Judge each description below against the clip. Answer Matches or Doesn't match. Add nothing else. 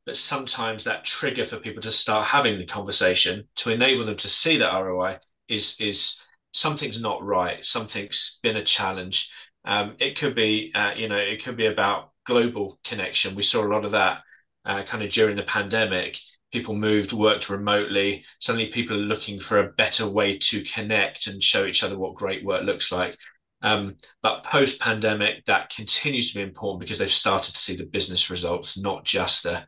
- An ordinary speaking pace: Matches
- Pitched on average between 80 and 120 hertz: Matches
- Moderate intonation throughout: Doesn't match